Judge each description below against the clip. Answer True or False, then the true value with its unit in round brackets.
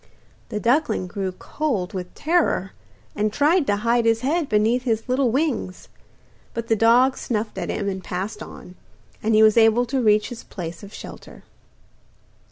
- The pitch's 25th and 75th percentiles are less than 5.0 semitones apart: True (3.7 semitones)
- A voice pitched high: True (225 Hz)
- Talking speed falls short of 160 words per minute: False (170 wpm)